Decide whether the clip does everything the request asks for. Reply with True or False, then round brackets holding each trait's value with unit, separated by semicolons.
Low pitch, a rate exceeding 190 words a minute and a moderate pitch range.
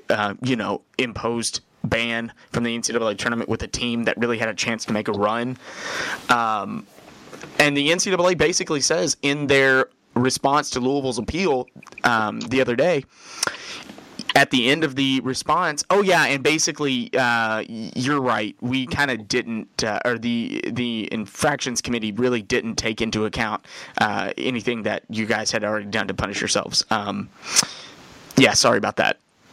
False (125 Hz; 165 wpm; 3.6 semitones)